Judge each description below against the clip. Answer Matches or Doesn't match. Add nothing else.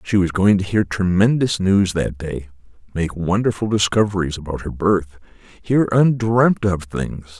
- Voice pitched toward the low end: Matches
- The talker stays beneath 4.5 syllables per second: Matches